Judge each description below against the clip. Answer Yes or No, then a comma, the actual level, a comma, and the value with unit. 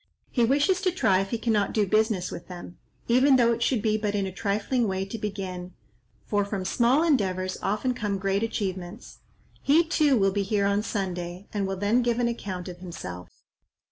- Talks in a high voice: Yes, high, 205 Hz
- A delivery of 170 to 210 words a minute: Yes, average, 200 wpm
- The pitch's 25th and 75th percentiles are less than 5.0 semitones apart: Yes, average, 3.8 semitones